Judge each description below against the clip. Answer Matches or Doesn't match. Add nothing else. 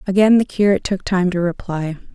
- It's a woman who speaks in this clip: Matches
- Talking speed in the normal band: Matches